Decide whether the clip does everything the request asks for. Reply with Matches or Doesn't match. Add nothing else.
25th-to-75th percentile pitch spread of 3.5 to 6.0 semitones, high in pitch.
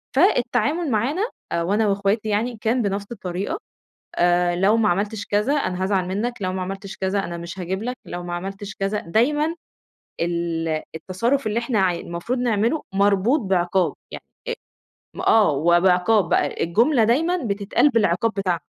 Matches